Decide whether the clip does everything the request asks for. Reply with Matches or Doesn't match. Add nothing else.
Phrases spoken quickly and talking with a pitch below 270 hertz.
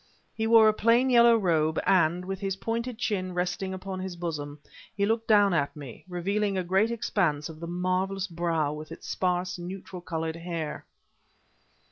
Doesn't match